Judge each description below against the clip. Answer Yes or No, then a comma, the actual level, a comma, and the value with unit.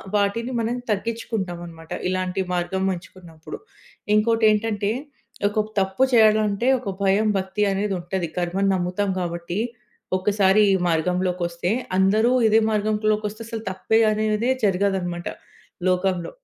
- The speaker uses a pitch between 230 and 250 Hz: No, high, 195 Hz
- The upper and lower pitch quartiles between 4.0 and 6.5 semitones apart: No, average, 2.9 semitones